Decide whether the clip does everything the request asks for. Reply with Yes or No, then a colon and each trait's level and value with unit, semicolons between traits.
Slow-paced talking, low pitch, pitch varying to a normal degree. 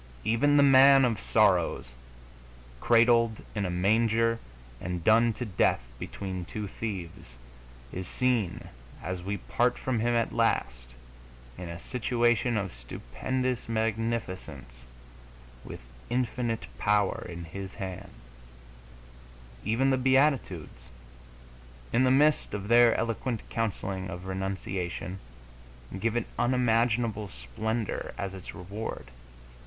Yes: slow, 115 wpm; low, 110 Hz; average, 4.3 semitones